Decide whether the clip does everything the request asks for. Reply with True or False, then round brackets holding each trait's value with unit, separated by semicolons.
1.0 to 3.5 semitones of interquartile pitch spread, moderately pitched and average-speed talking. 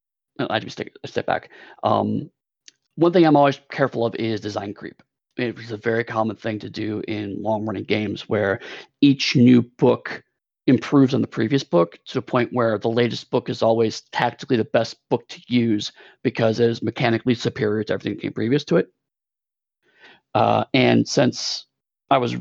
False (2.8 semitones; 115 Hz; 175 wpm)